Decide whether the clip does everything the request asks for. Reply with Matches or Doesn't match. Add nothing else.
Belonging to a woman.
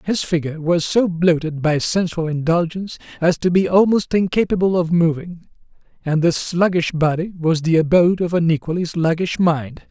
Doesn't match